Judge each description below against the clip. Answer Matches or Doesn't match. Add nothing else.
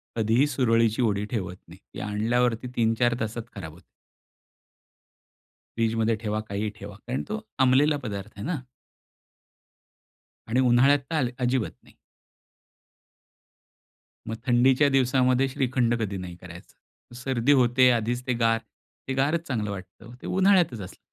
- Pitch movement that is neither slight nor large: Matches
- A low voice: Matches